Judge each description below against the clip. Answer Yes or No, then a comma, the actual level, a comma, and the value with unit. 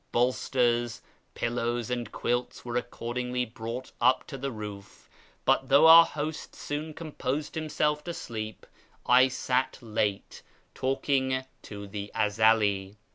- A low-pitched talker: Yes, low, 125 Hz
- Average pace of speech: No, slow, 130 wpm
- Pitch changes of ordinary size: Yes, average, 3.3 semitones